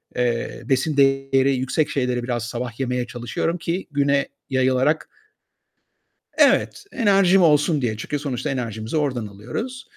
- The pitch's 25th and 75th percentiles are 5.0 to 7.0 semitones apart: No, average, 3.6 semitones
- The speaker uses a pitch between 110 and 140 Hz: Yes, low, 135 Hz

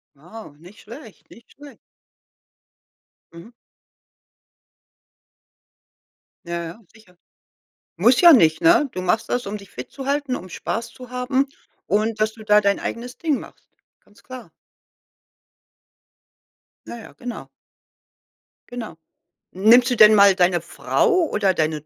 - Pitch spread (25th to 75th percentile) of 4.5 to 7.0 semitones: Yes, average, 5.1 semitones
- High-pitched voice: Yes, high, 220 Hz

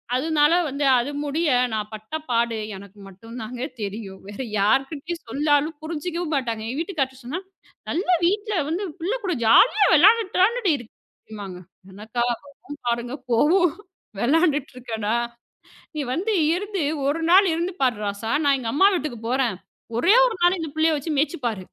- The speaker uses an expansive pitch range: Yes, wide, 6.5 semitones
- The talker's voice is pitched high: Yes, very high, 285 Hz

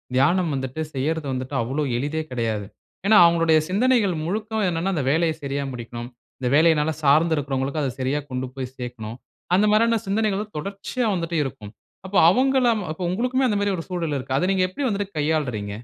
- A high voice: No, medium, 160 Hz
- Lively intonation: Yes, wide, 6.9 semitones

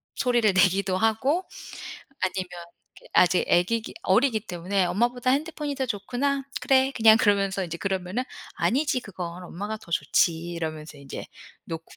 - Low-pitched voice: No, high, 200 Hz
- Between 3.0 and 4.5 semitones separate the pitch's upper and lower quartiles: No, wide, 5.5 semitones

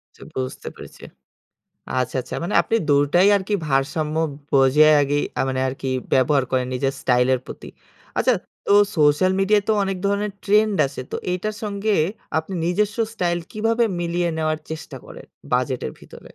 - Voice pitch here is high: No, medium, 160 Hz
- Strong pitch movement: Yes, wide, 6.8 semitones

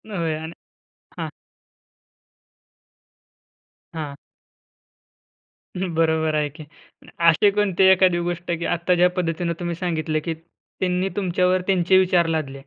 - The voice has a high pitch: No, medium, 175 Hz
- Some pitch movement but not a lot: No, narrow, 2.2 semitones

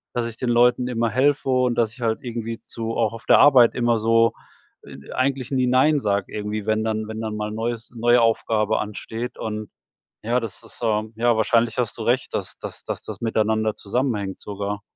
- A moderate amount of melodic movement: No, narrow, 2.0 semitones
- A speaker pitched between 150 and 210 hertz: No, low, 115 Hz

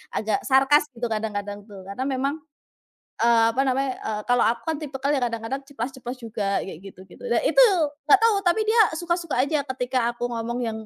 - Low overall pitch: No, very high, 250 Hz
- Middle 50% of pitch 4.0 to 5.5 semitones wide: Yes, average, 4.3 semitones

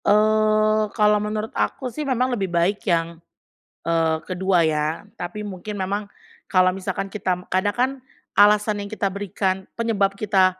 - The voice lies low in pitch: No, high, 200 Hz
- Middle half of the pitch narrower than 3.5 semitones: Yes, narrow, 2.5 semitones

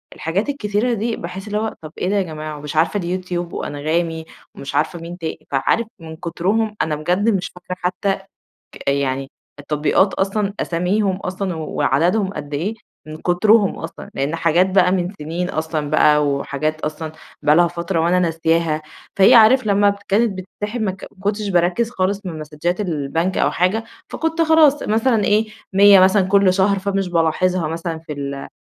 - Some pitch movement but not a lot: Yes, average, 4.1 semitones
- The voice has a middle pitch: Yes, medium, 180 Hz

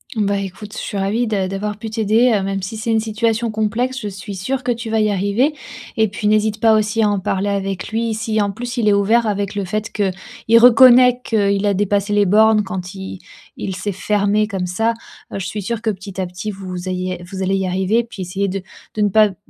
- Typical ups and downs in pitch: No, narrow, 2.3 semitones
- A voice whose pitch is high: Yes, high, 205 Hz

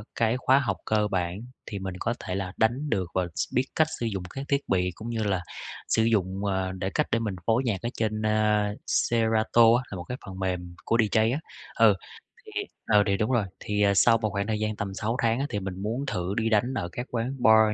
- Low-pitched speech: Yes, low, 110 Hz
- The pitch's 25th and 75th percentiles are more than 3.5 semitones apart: No, average, 3.2 semitones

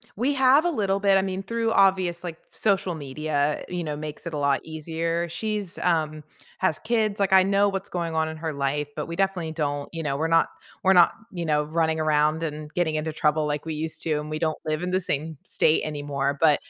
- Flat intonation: No, average, 3.8 semitones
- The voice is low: No, medium, 160 Hz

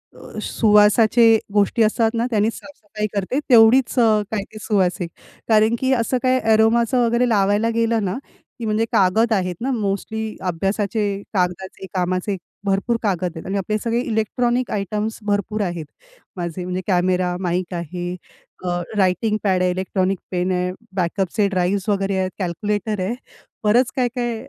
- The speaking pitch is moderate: No, high, 205 Hz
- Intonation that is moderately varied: Yes, average, 3.4 semitones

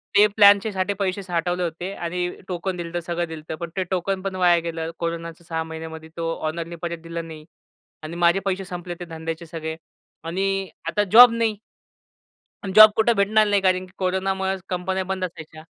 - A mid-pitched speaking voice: Yes, medium, 180 Hz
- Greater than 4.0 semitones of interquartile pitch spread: No, narrow, 2.5 semitones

